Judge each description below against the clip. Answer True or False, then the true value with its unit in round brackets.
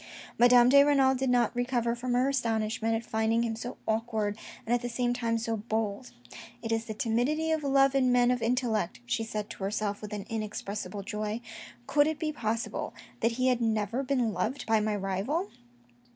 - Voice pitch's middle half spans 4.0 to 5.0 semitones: False (2.5 semitones)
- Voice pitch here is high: True (230 Hz)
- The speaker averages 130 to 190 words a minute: False (200 wpm)